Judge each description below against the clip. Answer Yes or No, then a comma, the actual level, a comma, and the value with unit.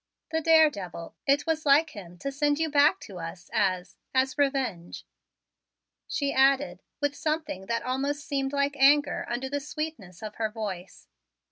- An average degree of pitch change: No, wide, 6.4 semitones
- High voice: Yes, very high, 275 Hz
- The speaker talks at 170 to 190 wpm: No, average, 155 wpm